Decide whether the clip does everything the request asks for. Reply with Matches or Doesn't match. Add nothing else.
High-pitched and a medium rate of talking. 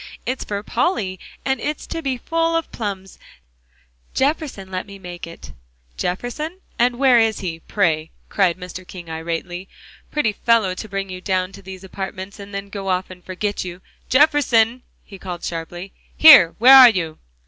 Matches